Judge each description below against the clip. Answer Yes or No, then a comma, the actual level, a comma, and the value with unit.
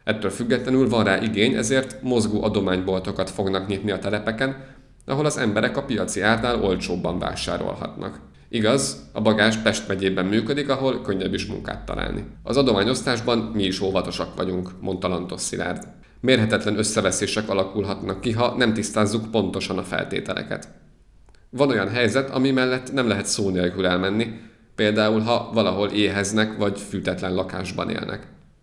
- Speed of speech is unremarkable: Yes, average, 145 wpm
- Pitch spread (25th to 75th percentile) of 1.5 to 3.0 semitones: No, average, 3.7 semitones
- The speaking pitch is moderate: No, low, 105 Hz